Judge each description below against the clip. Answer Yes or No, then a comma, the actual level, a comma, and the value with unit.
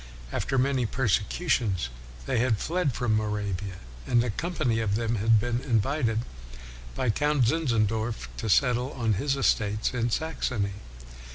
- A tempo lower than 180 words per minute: Yes, slow, 135 wpm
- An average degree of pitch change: Yes, average, 3.8 semitones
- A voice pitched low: Yes, low, 115 Hz